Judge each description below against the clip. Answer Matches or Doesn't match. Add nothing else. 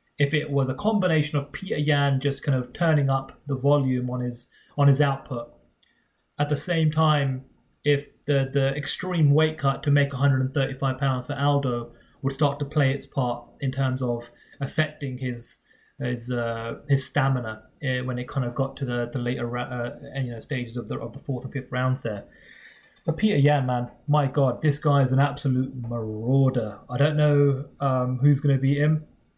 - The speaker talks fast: Doesn't match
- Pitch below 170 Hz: Matches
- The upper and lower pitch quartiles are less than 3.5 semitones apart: Matches